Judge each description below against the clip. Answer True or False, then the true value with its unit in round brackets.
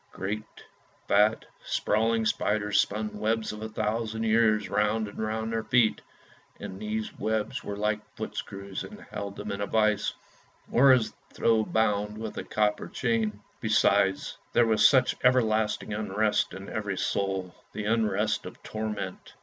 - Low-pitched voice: True (110 Hz)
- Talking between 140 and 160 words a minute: True (150 wpm)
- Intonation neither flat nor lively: False (1.3 semitones)